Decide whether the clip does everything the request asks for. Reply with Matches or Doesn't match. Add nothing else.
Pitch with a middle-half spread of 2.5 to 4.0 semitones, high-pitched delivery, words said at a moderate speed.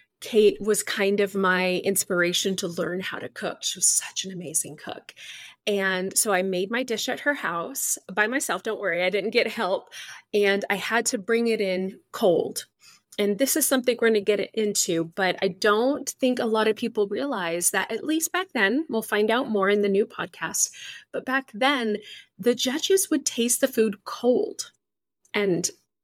Doesn't match